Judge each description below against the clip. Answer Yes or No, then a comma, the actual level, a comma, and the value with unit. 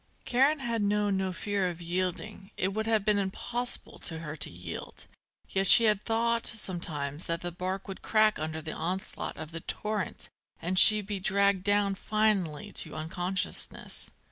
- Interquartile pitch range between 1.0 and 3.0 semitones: No, average, 3.5 semitones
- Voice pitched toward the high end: Yes, high, 195 Hz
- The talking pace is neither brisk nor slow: Yes, average, 170 wpm